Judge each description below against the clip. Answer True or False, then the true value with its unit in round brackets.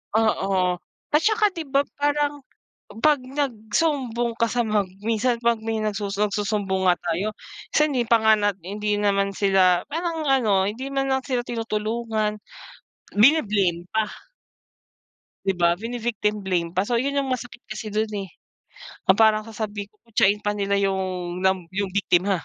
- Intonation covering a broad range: False (3.5 semitones)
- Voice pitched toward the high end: True (215 Hz)